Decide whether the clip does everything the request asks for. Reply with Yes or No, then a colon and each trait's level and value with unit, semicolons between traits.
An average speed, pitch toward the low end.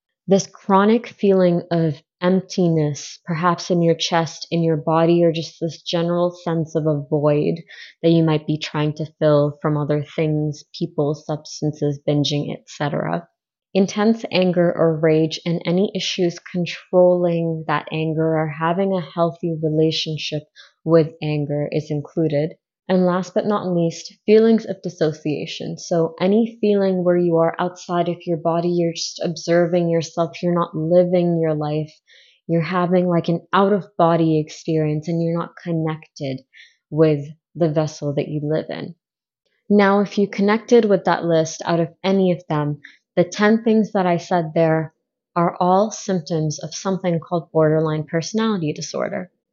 No: average, 155 wpm; medium, 170 Hz